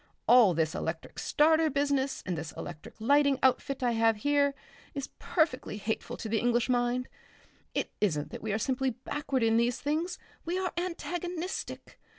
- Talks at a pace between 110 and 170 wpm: Yes, average, 160 wpm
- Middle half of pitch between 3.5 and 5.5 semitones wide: Yes, average, 4.6 semitones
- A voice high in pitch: Yes, very high, 255 Hz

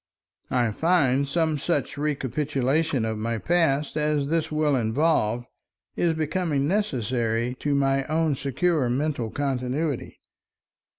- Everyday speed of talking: No, slow, 115 wpm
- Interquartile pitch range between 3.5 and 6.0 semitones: Yes, average, 3.9 semitones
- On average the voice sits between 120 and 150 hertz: Yes, medium, 140 Hz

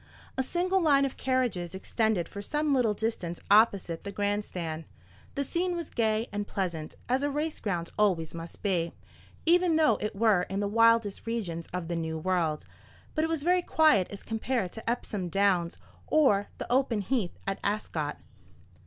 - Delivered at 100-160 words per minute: No, average, 175 wpm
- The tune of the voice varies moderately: No, wide, 6.6 semitones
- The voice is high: Yes, high, 210 Hz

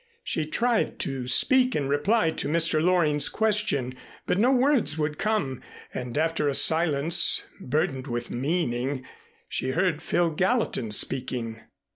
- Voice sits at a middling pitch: Yes, medium, 155 Hz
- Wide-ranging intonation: Yes, wide, 5.7 semitones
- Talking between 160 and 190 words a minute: No, slow, 135 wpm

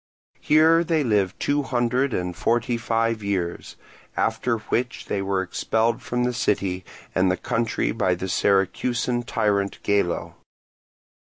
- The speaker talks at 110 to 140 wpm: Yes, slow, 135 wpm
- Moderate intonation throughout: Yes, average, 4.1 semitones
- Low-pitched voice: Yes, low, 110 Hz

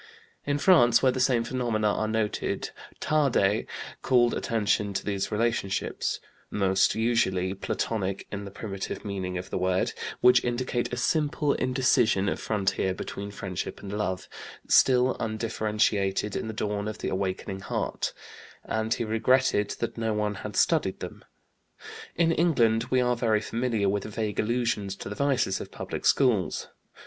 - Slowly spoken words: No, average, 150 wpm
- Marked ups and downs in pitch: No, average, 3.7 semitones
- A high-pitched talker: No, low, 110 Hz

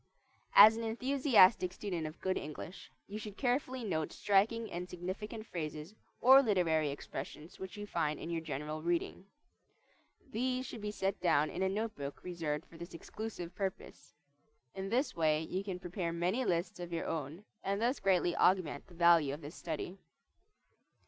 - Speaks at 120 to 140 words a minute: No, average, 170 wpm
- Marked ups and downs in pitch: No, average, 4.3 semitones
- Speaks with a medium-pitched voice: Yes, medium, 180 Hz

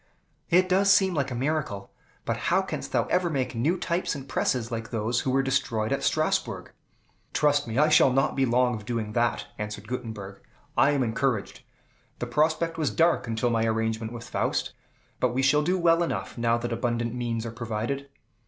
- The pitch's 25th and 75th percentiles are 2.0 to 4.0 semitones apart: No, average, 4.5 semitones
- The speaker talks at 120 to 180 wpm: No, average, 190 wpm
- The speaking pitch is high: No, low, 125 Hz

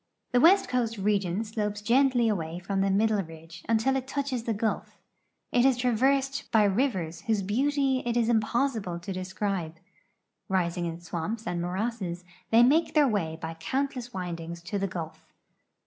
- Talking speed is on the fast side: No, average, 165 wpm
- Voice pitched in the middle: No, high, 210 Hz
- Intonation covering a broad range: Yes, wide, 5.7 semitones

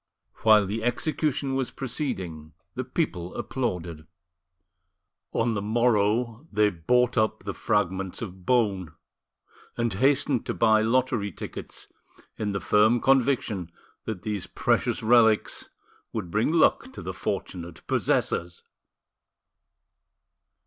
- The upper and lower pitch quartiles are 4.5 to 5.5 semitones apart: No, average, 4.1 semitones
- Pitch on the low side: Yes, low, 110 Hz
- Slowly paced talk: Yes, slow, 115 wpm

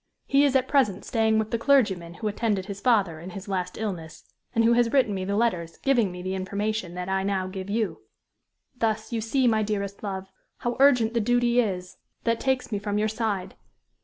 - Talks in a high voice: Yes, high, 215 Hz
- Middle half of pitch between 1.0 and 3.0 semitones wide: No, average, 3.5 semitones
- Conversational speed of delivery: No, fast, 210 wpm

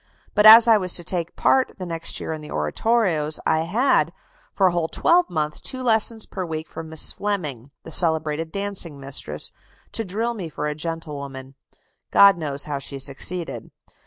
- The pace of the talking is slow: No, average, 180 wpm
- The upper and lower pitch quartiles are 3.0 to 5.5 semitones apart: Yes, average, 5.1 semitones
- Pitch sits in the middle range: Yes, medium, 165 Hz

